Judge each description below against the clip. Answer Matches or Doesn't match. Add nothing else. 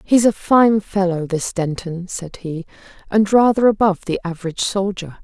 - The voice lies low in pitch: Doesn't match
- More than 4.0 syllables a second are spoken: Matches